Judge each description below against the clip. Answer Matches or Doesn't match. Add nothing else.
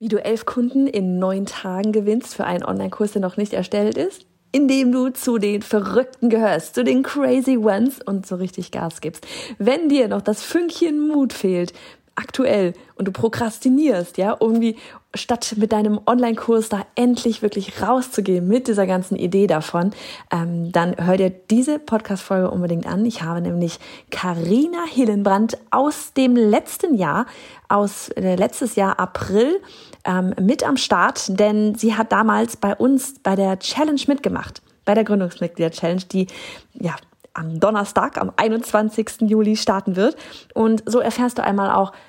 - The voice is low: Doesn't match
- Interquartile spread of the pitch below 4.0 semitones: Doesn't match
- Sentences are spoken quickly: Doesn't match